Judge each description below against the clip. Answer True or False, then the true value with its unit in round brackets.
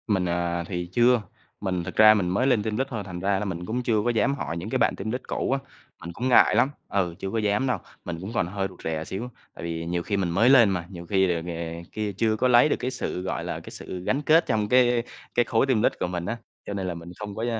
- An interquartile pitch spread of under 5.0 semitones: False (5.3 semitones)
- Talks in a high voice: False (100 Hz)